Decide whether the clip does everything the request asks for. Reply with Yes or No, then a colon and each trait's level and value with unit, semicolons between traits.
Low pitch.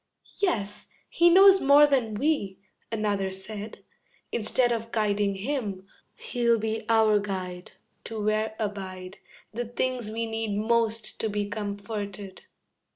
No: high, 215 Hz